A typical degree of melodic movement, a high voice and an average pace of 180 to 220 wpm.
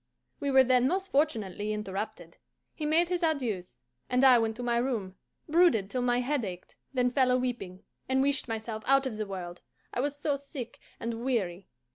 Yes: average, 4.3 semitones; high, 245 Hz; average, 190 wpm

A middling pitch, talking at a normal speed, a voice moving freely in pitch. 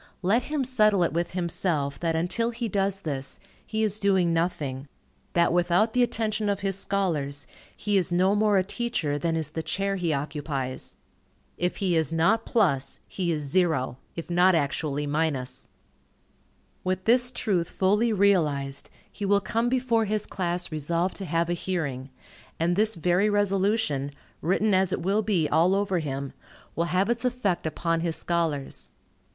No: medium, 180 Hz; average, 165 wpm; average, 4.3 semitones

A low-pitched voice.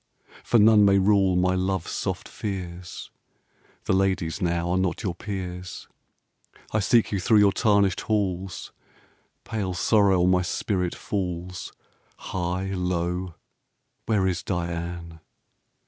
Yes: very low, 95 Hz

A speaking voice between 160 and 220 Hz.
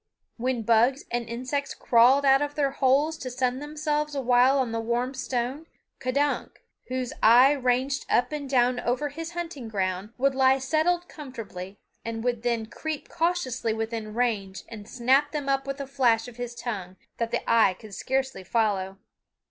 No: very high, 255 Hz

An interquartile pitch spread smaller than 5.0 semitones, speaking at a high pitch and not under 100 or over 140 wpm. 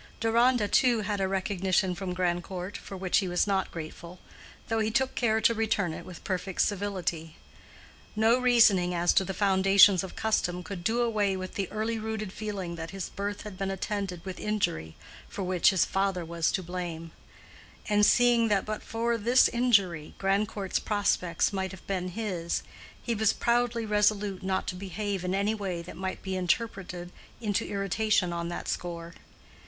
No: average, 3.0 semitones; high, 195 Hz; average, 175 wpm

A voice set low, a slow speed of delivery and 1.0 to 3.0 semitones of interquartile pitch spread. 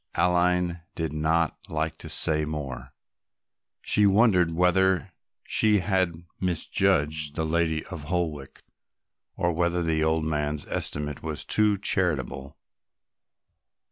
Yes: very low, 80 Hz; slow, 110 wpm; average, 2.7 semitones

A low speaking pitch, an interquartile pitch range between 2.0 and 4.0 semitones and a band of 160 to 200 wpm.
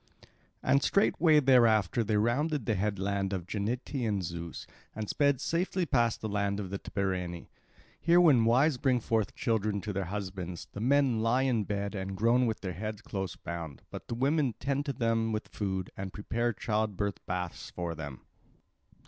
No: low, 110 Hz; average, 4.5 semitones; average, 170 wpm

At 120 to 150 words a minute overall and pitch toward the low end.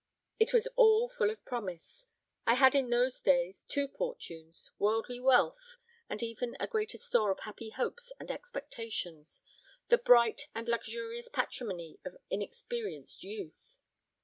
No: average, 140 wpm; very high, 255 Hz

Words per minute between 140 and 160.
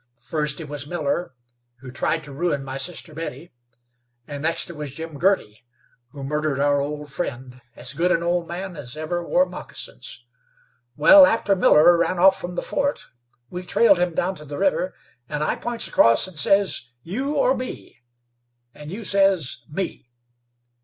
No: average, 170 wpm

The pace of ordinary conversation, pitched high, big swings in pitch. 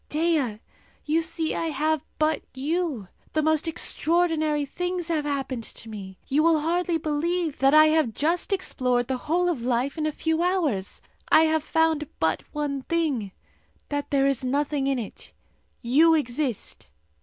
No: average, 160 wpm; very high, 305 Hz; average, 3.3 semitones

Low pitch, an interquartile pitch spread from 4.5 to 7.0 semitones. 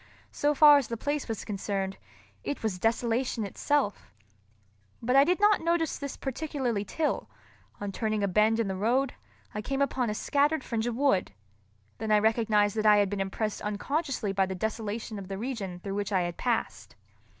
No: high, 225 Hz; average, 5.0 semitones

